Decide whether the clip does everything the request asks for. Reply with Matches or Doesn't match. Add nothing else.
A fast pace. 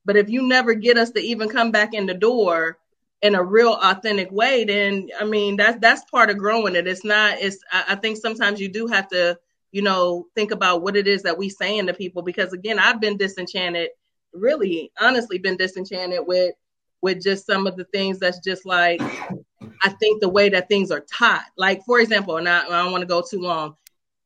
Matches